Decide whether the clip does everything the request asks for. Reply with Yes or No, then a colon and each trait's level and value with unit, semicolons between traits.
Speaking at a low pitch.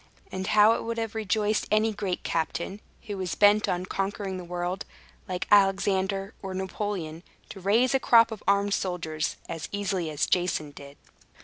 No: high, 195 Hz